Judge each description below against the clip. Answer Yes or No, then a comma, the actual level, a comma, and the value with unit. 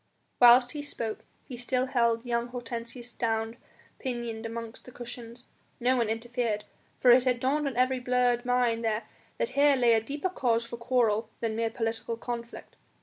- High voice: Yes, high, 240 Hz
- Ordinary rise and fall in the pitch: No, narrow, 1.6 semitones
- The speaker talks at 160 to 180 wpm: Yes, average, 170 wpm